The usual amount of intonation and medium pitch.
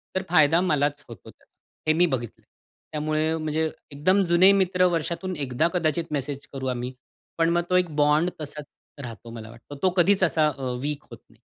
Yes: average, 3.7 semitones; medium, 155 Hz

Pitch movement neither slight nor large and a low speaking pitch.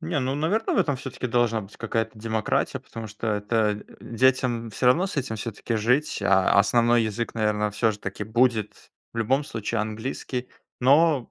Yes: average, 3.2 semitones; low, 115 Hz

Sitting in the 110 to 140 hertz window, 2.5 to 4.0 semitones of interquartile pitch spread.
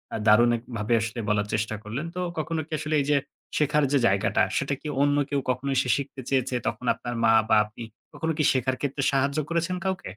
No: low, 135 Hz; average, 4.5 semitones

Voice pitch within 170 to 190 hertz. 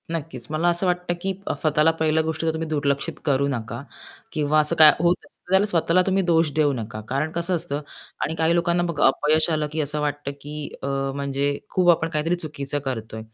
No: medium, 155 Hz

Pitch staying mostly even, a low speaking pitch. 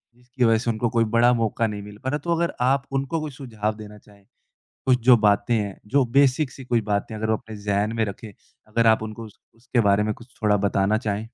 No: average, 3.2 semitones; low, 115 Hz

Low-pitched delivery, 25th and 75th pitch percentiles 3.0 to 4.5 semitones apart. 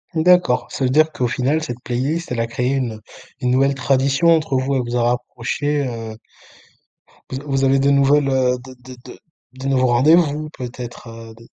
No: low, 130 Hz; narrow, 2.5 semitones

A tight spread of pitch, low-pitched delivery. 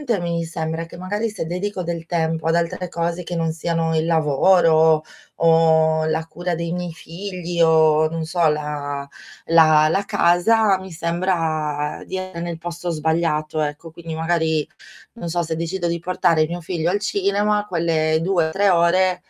No: narrow, 2.0 semitones; medium, 170 Hz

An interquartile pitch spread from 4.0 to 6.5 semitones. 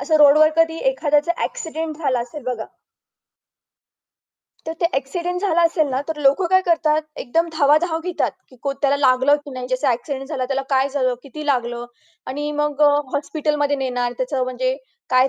No: average, 3.3 semitones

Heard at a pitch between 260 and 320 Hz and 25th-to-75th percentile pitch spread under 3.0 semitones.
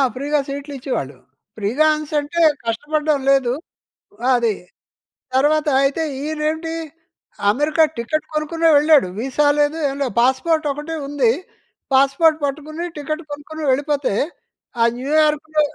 Yes: very high, 295 Hz; narrow, 2.4 semitones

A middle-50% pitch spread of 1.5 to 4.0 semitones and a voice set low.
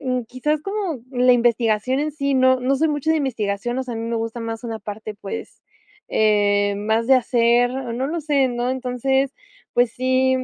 No: average, 2.7 semitones; very high, 250 Hz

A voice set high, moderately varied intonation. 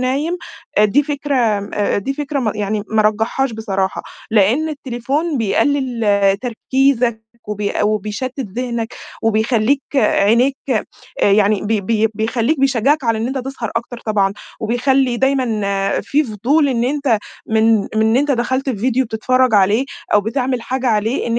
Yes: high, 235 Hz; average, 3.7 semitones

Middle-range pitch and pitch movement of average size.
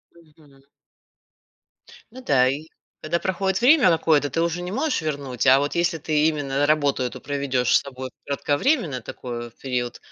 Yes: medium, 145 Hz; average, 4.1 semitones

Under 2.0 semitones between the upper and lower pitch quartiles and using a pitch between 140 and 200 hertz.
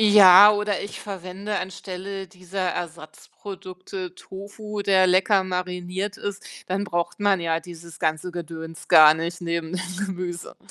No: narrow, 2.4 semitones; medium, 185 Hz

